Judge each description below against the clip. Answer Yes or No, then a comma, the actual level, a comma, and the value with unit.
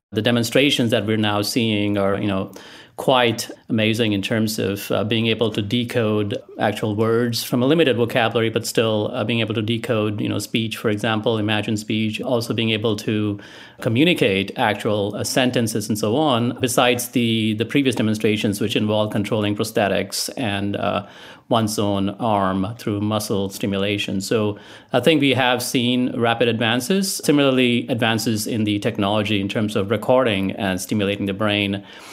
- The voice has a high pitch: No, low, 110 Hz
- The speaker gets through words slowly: No, average, 165 wpm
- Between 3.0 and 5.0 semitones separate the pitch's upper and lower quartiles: No, narrow, 2.6 semitones